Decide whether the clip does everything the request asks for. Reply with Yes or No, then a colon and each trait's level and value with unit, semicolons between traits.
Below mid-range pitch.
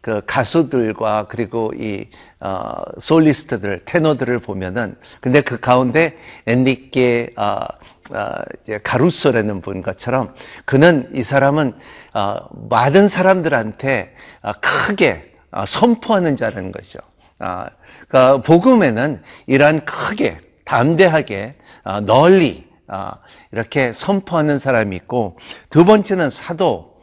Yes: low, 130 Hz